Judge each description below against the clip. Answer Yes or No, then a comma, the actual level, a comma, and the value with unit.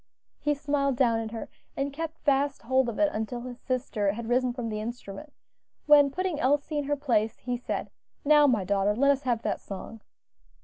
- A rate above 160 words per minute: Yes, average, 195 wpm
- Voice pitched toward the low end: No, very high, 255 Hz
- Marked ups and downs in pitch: No, average, 4.1 semitones